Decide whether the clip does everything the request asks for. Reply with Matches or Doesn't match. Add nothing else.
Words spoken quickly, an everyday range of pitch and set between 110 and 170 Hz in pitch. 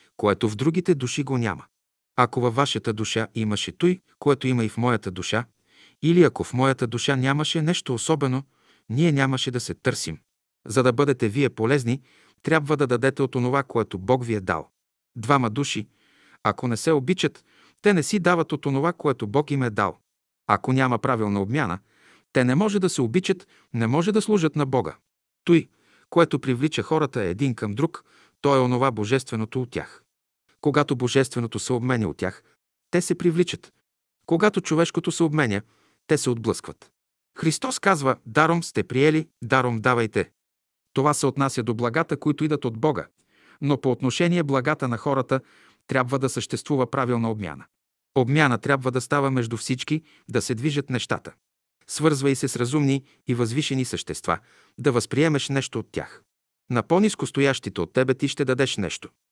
Matches